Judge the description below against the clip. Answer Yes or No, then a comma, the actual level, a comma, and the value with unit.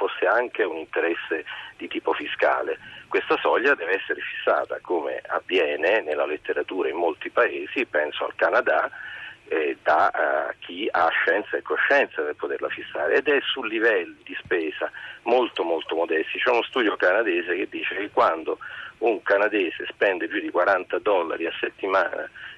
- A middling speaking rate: Yes, average, 155 wpm